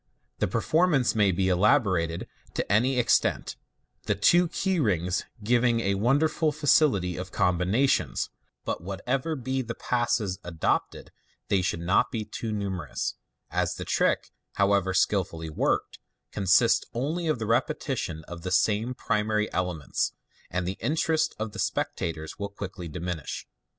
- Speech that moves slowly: No, average, 145 wpm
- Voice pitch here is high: No, low, 105 Hz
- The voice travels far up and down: Yes, wide, 5.7 semitones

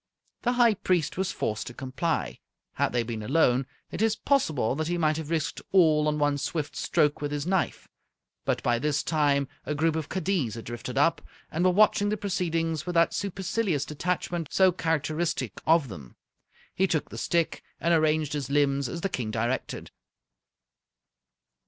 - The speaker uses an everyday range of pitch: Yes, average, 3.9 semitones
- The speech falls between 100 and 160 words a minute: No, average, 175 wpm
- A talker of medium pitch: Yes, medium, 155 Hz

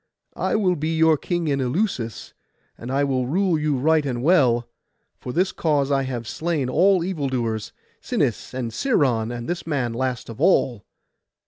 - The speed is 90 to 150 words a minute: No, average, 165 wpm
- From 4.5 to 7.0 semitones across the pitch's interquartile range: Yes, average, 5.2 semitones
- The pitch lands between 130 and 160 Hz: Yes, medium, 140 Hz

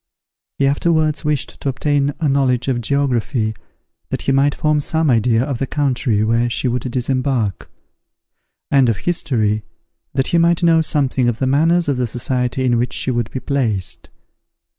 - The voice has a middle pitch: No, low, 130 Hz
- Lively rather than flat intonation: No, average, 3.1 semitones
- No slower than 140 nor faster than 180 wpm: Yes, average, 170 wpm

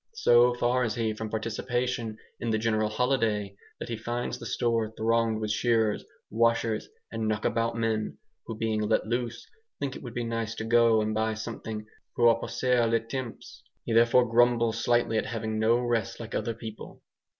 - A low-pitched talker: Yes, low, 115 Hz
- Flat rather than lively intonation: Yes, narrow, 1.4 semitones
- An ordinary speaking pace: Yes, average, 180 wpm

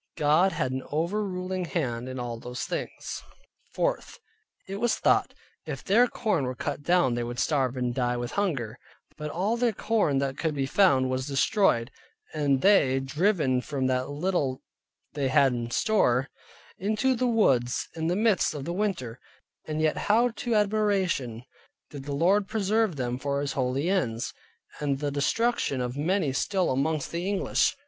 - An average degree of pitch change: No, wide, 7.0 semitones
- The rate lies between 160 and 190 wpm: Yes, average, 170 wpm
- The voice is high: No, medium, 150 Hz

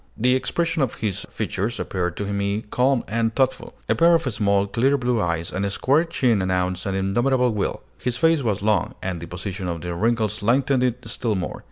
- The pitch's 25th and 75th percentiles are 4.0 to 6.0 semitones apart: Yes, average, 4.7 semitones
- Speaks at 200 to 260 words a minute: Yes, fast, 205 wpm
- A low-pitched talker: Yes, low, 110 Hz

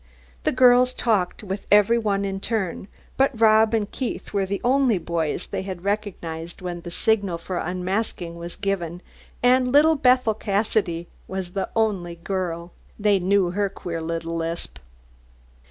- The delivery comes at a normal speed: Yes, average, 155 wpm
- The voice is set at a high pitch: Yes, high, 195 Hz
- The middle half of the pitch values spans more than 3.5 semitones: Yes, average, 4.1 semitones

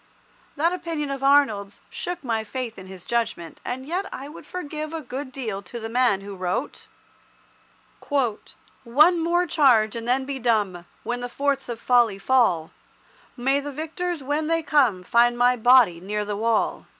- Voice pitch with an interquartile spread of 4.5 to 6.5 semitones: Yes, average, 5.0 semitones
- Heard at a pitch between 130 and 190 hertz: No, very high, 250 Hz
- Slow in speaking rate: No, average, 170 wpm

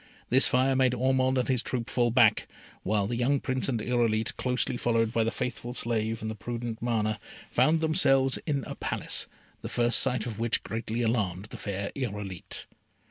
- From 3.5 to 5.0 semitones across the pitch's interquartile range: No, average, 2.7 semitones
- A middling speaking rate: Yes, average, 185 wpm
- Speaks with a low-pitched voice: Yes, low, 120 Hz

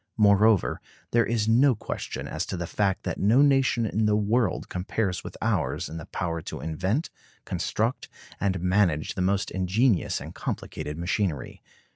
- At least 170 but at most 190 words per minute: No, average, 160 wpm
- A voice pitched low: Yes, low, 100 Hz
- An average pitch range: Yes, average, 3.8 semitones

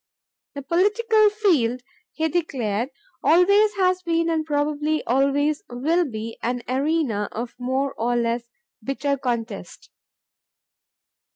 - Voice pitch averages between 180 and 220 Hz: No, very high, 280 Hz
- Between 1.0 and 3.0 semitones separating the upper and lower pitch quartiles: No, wide, 5.5 semitones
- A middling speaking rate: No, slow, 110 wpm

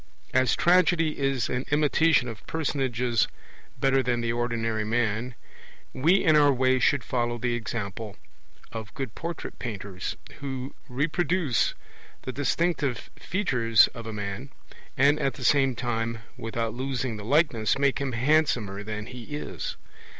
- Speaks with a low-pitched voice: Yes, low, 125 Hz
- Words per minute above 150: No, average, 140 wpm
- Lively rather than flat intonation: No, average, 3.7 semitones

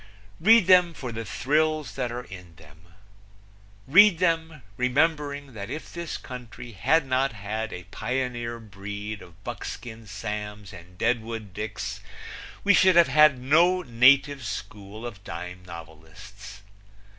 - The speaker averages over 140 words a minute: No, slow, 135 wpm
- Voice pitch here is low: Yes, low, 120 Hz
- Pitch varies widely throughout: Yes, wide, 6.4 semitones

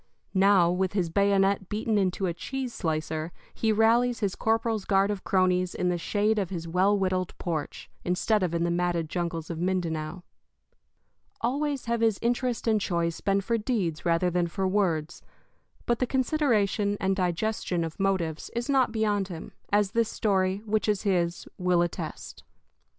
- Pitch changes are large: No, average, 3.8 semitones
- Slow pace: No, average, 165 wpm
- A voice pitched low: No, high, 195 Hz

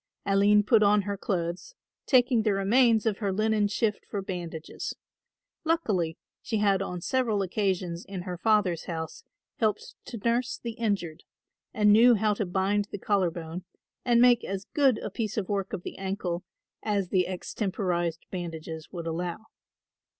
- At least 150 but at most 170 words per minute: Yes, average, 160 wpm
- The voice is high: Yes, high, 200 Hz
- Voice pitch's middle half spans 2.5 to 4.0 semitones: Yes, average, 3.4 semitones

